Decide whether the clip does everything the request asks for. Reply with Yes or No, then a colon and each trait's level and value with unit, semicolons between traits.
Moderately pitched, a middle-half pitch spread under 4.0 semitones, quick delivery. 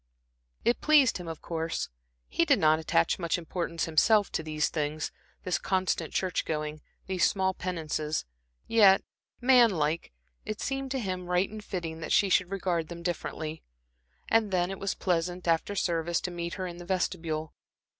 No: medium, 175 Hz; average, 3.0 semitones; average, 165 wpm